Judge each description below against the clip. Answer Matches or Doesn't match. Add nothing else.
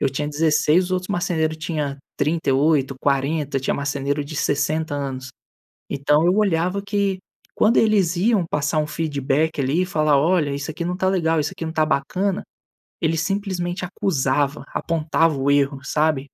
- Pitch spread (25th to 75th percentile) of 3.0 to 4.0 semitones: Matches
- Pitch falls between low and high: Matches